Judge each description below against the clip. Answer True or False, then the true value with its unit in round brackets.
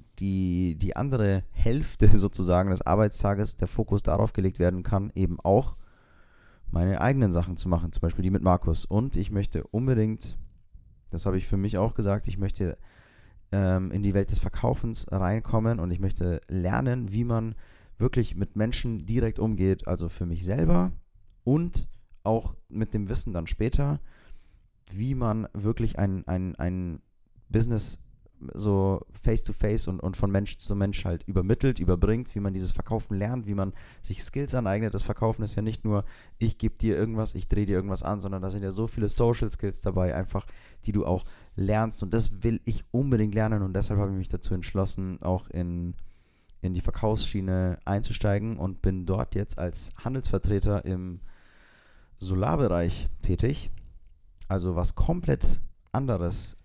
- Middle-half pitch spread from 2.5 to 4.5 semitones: True (3.2 semitones)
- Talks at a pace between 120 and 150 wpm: False (165 wpm)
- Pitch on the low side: True (100 Hz)